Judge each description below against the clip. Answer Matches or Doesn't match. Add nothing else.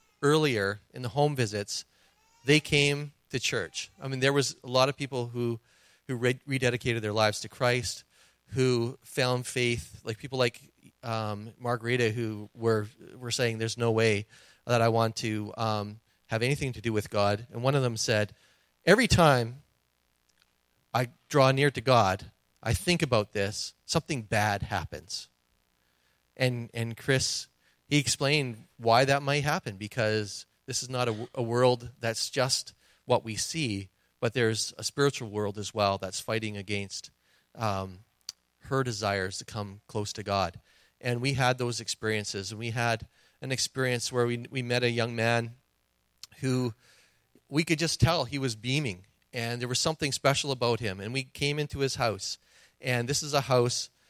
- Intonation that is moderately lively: Matches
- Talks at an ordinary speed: Matches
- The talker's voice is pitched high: Doesn't match